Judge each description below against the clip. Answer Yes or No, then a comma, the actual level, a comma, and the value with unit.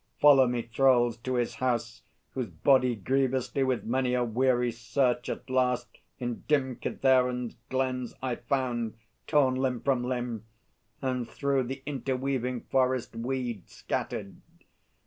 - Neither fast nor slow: No, slow, 130 wpm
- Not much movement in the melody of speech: Yes, narrow, 1.5 semitones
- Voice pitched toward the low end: Yes, low, 125 Hz